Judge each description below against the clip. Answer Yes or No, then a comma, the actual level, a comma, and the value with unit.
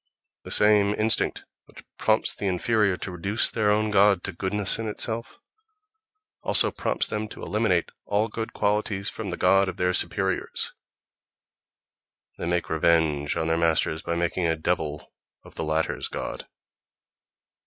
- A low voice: Yes, very low, 95 Hz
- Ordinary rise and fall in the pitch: Yes, average, 3.8 semitones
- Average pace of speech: Yes, average, 150 wpm